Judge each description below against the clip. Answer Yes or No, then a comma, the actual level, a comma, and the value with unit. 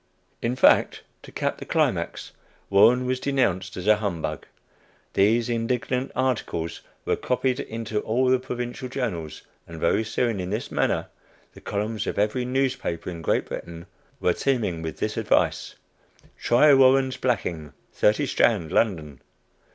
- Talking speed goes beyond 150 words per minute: No, average, 145 wpm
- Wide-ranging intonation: Yes, wide, 5.7 semitones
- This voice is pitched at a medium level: No, low, 115 Hz